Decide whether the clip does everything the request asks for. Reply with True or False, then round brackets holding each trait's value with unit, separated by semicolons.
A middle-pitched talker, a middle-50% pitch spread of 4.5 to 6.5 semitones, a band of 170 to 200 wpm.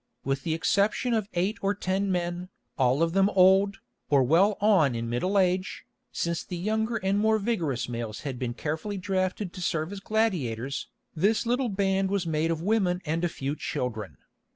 True (180 Hz; 4.8 semitones; 180 wpm)